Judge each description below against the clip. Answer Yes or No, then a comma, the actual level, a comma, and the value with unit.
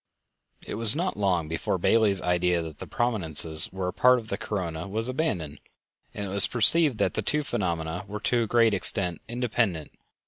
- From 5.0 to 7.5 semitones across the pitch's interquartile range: Yes, average, 5.3 semitones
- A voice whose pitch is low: Yes, low, 100 Hz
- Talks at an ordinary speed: Yes, average, 185 wpm